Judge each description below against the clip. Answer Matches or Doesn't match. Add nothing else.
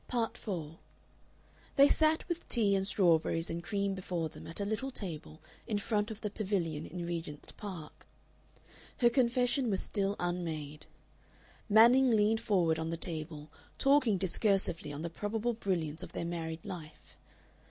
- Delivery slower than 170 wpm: Matches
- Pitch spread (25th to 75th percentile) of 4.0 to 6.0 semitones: Matches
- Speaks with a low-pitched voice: Doesn't match